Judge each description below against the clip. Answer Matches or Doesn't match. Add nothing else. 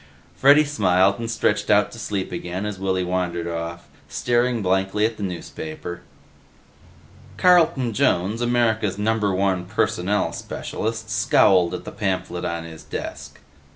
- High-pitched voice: Doesn't match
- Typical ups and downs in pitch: Matches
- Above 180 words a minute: Doesn't match